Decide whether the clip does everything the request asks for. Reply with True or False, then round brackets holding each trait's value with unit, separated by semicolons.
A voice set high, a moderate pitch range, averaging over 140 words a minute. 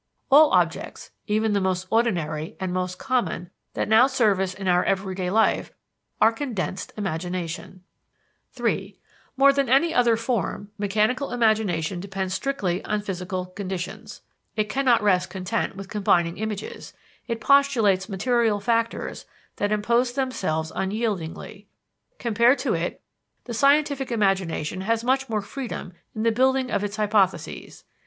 False (210 Hz; 4.1 semitones; 135 wpm)